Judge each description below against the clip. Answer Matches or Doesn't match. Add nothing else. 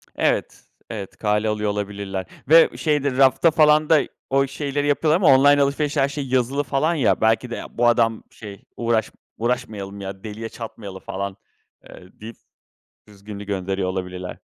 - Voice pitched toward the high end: Doesn't match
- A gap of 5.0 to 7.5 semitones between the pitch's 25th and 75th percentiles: Matches